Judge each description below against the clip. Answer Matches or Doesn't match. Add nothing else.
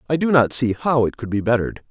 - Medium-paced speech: Doesn't match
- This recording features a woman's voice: Doesn't match